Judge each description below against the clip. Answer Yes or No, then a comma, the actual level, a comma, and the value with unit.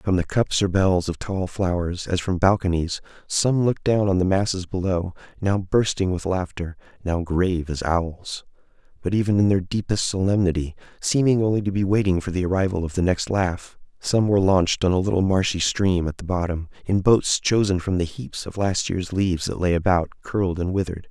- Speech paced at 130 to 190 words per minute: No, average, 200 wpm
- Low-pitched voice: Yes, very low, 95 Hz